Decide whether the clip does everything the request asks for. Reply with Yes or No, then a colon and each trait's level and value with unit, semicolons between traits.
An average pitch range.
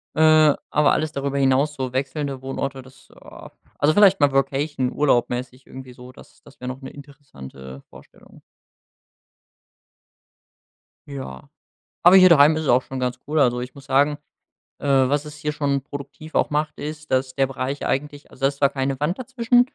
No: narrow, 2.3 semitones